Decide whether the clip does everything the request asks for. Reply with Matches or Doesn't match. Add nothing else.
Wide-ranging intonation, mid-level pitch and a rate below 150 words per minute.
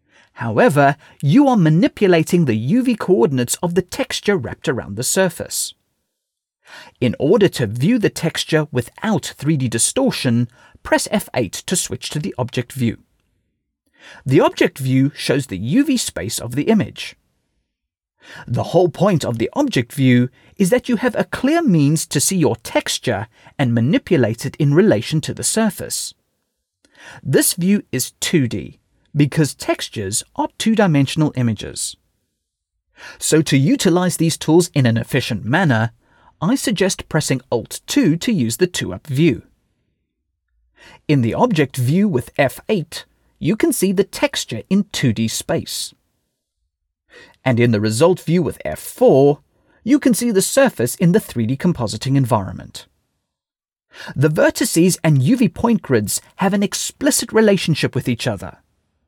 Matches